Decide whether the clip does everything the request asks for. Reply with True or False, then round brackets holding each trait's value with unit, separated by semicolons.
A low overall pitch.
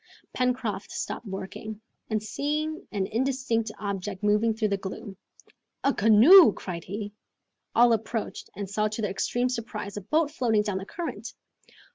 False (215 Hz)